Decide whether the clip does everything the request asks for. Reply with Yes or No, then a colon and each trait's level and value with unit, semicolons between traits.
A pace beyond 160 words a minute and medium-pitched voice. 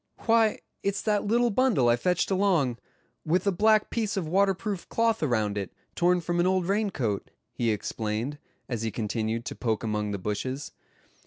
Yes: average, 175 wpm; medium, 170 Hz